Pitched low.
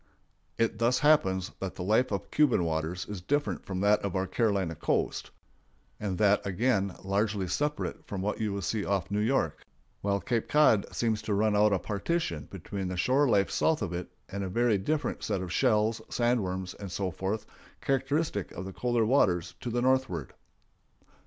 Yes: low, 105 Hz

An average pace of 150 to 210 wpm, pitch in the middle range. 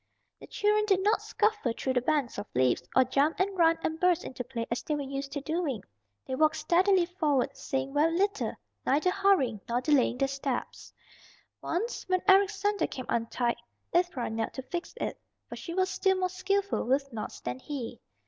No: average, 190 wpm; very high, 305 Hz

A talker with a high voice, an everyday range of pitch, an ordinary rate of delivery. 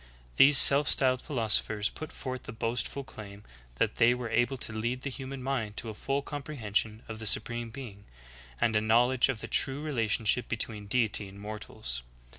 No: low, 115 Hz; average, 3.6 semitones; average, 190 wpm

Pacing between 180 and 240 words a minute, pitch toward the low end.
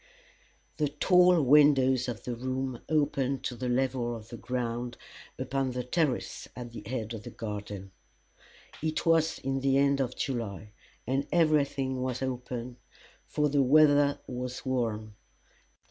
No: average, 145 wpm; low, 130 Hz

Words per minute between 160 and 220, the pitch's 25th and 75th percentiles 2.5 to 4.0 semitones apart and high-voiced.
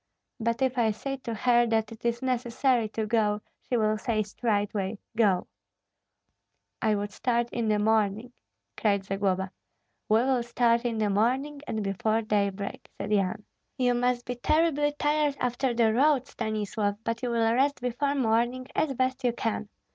Yes: average, 165 wpm; average, 2.8 semitones; high, 230 Hz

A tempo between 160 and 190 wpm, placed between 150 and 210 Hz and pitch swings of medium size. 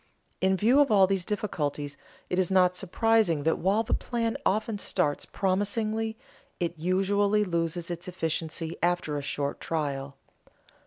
No: average, 145 wpm; medium, 185 Hz; average, 4.2 semitones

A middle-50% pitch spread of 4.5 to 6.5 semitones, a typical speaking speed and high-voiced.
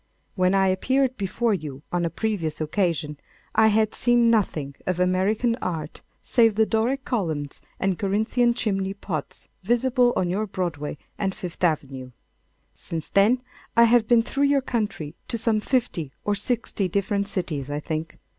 Yes: wide, 5.6 semitones; average, 155 wpm; high, 195 Hz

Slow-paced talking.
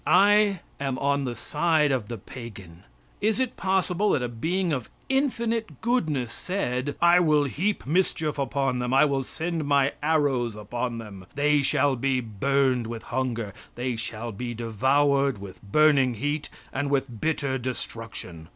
No: average, 155 wpm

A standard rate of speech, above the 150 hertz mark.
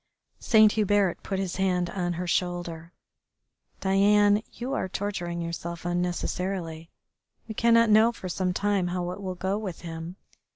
Yes: average, 150 wpm; medium, 185 Hz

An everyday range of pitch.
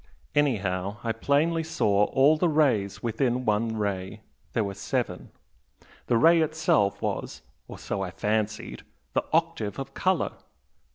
No: wide, 6.9 semitones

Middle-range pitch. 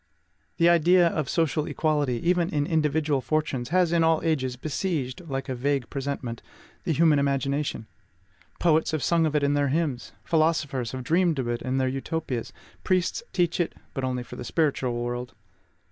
Yes: medium, 145 Hz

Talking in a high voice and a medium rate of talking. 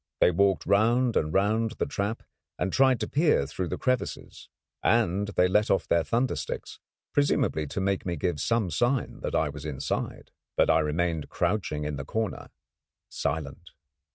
No: very low, 95 Hz; average, 170 wpm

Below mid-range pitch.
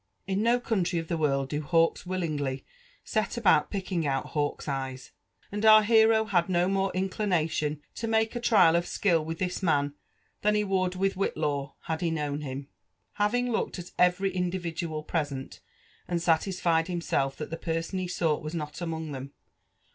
No: medium, 170 Hz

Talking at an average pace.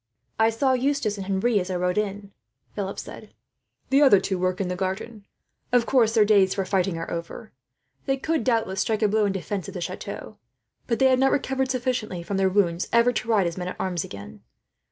No: fast, 215 wpm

